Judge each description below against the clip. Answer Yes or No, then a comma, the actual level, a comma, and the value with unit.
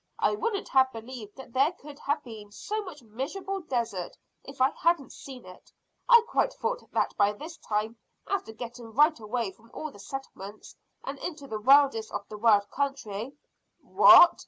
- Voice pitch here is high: Yes, very high, 260 Hz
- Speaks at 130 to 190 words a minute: Yes, average, 175 wpm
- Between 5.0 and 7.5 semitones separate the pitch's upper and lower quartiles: Yes, wide, 5.5 semitones